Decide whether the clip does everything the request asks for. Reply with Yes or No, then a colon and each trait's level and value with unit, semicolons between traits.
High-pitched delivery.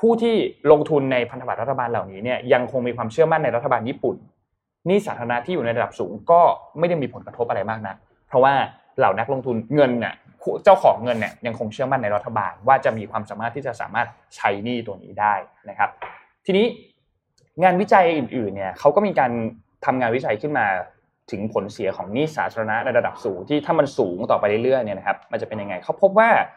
No: low, 125 Hz